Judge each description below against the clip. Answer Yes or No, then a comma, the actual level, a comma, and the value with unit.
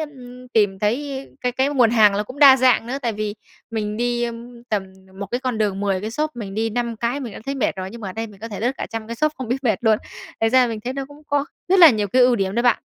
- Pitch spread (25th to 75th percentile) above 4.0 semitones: No, average, 3.3 semitones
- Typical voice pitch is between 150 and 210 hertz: No, high, 235 Hz